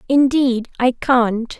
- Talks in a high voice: Yes, very high, 250 Hz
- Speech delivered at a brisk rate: No, slow, 115 wpm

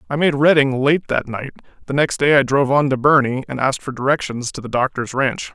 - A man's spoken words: Yes, male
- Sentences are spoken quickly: Yes, fast, 240 wpm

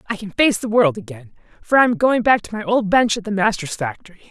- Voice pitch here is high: Yes, high, 225 Hz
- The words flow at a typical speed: No, fast, 250 wpm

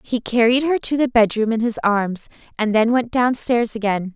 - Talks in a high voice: Yes, high, 230 Hz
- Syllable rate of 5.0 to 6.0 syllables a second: No, 4.8 syllables/s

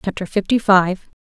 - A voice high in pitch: Yes, high, 195 Hz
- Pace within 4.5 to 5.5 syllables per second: Yes, 4.9 syllables/s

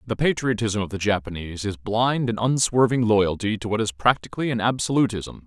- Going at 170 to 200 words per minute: Yes, average, 175 wpm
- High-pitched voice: No, low, 110 Hz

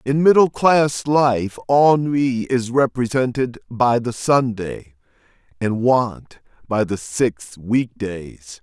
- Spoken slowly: Yes, slow, 120 wpm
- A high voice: No, low, 125 Hz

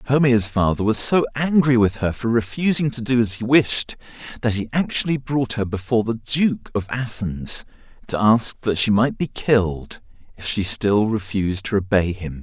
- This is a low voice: Yes, low, 110 Hz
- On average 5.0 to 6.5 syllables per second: No, 4.8 syllables/s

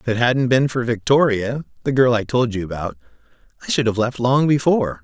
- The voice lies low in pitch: Yes, low, 120 Hz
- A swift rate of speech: No, average, 190 wpm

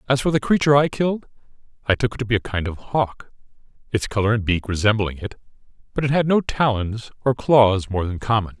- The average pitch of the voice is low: Yes, low, 115 Hz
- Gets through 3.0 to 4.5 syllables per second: No, 5.9 syllables/s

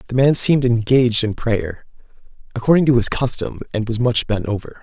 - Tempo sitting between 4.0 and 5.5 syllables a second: No, 5.8 syllables/s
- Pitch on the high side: No, low, 120 Hz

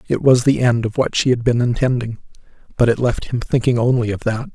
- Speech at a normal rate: No, fast, 240 wpm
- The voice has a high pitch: No, low, 125 Hz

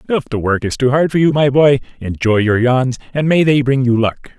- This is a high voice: No, low, 130 Hz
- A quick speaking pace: Yes, fast, 260 wpm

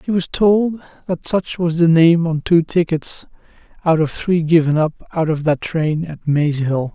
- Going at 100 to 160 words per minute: No, average, 200 wpm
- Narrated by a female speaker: No, male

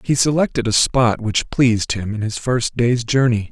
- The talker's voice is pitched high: No, low, 120 Hz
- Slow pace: No, fast, 205 wpm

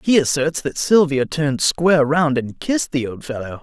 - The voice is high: No, medium, 145 Hz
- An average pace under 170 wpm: No, average, 200 wpm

